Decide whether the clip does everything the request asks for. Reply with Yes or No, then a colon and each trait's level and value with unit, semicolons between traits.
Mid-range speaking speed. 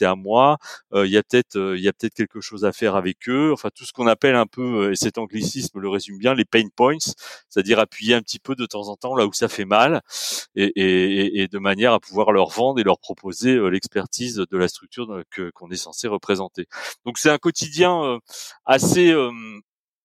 No: fast, 235 wpm